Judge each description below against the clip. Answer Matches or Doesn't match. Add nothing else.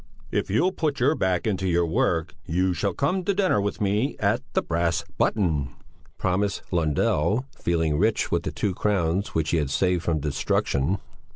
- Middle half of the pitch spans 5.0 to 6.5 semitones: Doesn't match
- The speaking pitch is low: Matches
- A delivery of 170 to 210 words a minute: Matches